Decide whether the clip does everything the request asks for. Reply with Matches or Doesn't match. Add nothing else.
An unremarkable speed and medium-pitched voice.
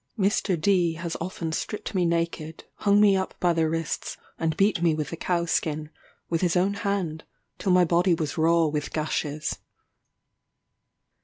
Matches